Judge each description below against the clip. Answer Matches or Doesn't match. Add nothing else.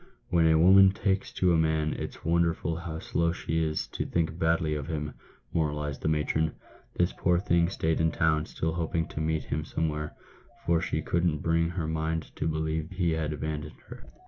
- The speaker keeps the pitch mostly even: Matches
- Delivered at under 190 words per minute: Doesn't match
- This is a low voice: Matches